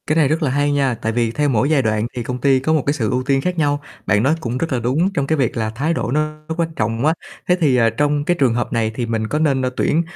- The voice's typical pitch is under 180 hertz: Yes, low, 135 Hz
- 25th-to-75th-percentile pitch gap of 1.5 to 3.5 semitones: No, average, 4.4 semitones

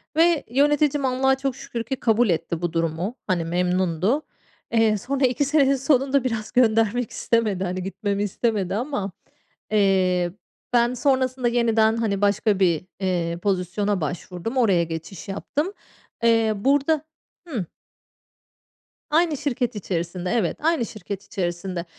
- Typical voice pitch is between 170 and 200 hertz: No, high, 220 Hz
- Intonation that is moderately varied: No, wide, 5.9 semitones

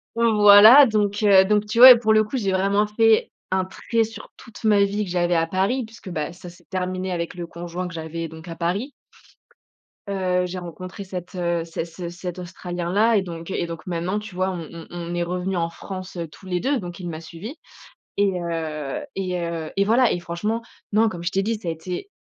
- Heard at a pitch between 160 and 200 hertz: Yes, medium, 185 Hz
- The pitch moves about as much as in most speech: Yes, average, 3.4 semitones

